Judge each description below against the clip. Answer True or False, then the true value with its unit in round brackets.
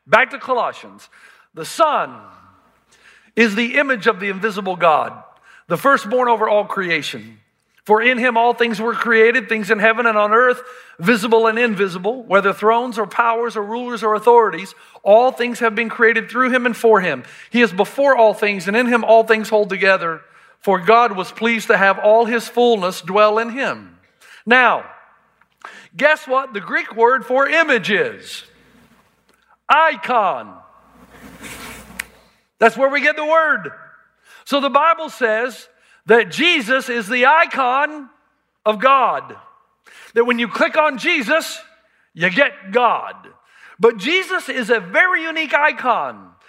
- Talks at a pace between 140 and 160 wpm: True (150 wpm)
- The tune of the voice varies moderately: True (3.4 semitones)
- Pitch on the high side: True (235 Hz)